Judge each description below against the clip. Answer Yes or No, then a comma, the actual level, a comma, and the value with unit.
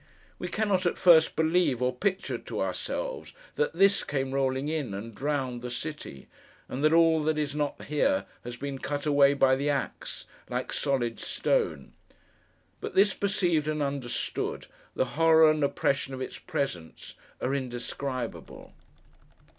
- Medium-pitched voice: Yes, medium, 145 Hz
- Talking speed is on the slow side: No, average, 150 wpm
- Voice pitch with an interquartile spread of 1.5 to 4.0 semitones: Yes, average, 3.6 semitones